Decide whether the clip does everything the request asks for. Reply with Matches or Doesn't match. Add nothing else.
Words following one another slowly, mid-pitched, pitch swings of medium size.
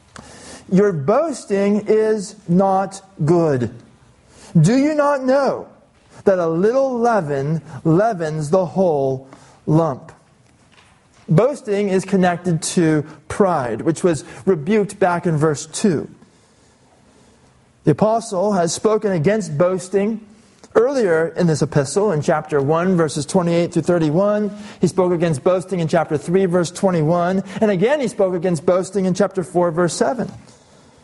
Matches